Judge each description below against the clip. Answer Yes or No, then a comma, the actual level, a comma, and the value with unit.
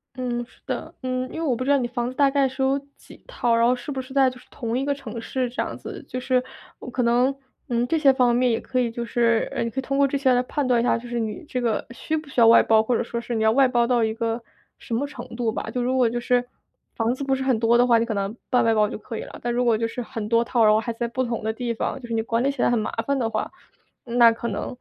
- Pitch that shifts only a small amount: Yes, narrow, 2.0 semitones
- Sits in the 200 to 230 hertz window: No, high, 240 Hz